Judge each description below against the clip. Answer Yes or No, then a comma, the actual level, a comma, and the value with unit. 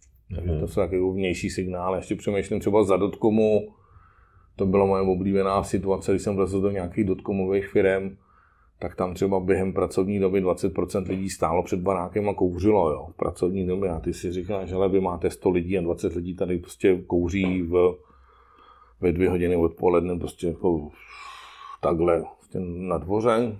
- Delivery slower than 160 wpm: No, average, 165 wpm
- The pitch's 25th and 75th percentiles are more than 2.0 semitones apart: No, narrow, 1.7 semitones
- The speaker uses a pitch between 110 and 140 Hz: No, very low, 95 Hz